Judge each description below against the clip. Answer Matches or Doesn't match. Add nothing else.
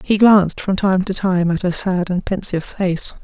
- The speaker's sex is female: Matches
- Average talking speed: Doesn't match